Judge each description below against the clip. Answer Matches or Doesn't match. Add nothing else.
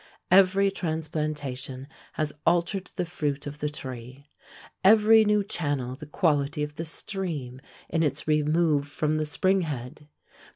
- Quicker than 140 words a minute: Doesn't match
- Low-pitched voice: Doesn't match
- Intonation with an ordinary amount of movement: Matches